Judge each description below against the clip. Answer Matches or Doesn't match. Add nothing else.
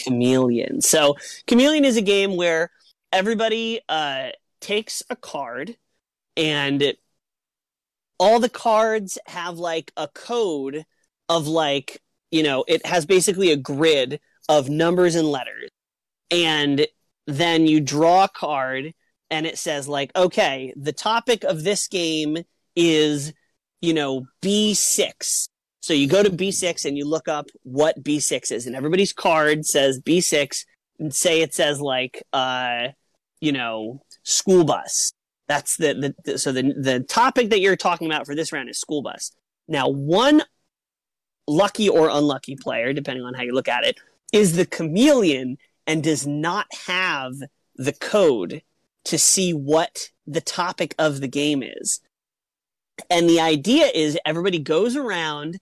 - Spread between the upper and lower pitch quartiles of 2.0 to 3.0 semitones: Doesn't match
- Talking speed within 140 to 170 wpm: Matches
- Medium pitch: Matches